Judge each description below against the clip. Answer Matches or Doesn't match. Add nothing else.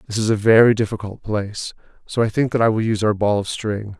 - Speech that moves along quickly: Matches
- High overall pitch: Doesn't match